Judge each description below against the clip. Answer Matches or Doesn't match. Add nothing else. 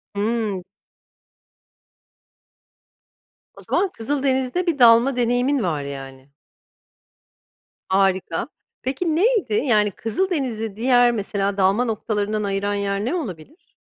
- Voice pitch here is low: Doesn't match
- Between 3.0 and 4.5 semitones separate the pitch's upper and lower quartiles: Doesn't match